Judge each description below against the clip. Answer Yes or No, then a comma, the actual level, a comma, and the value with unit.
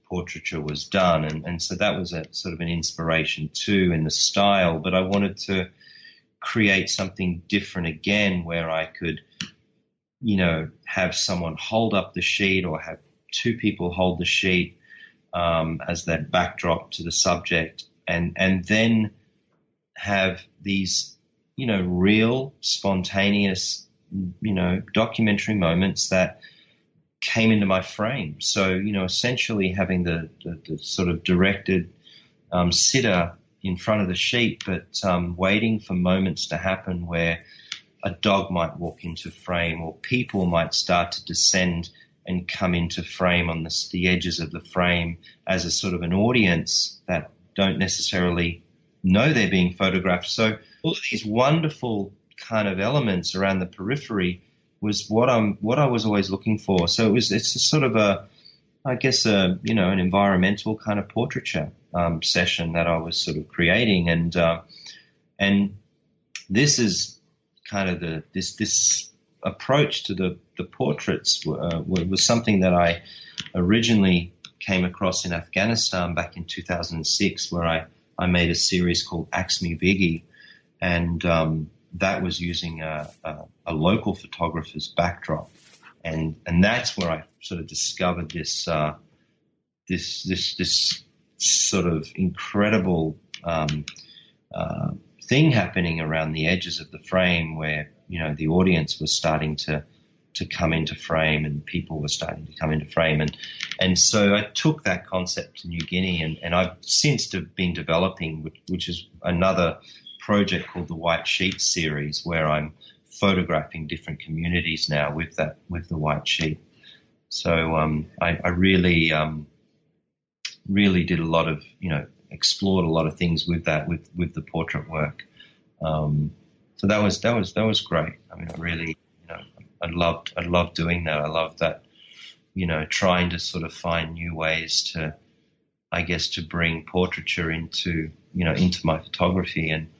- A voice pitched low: Yes, very low, 90 Hz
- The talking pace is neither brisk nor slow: Yes, average, 160 wpm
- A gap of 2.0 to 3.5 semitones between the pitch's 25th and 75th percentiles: Yes, average, 2.9 semitones